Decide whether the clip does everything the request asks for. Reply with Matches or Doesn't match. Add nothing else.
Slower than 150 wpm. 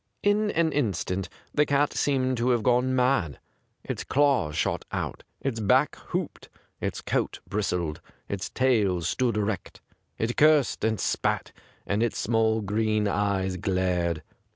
Matches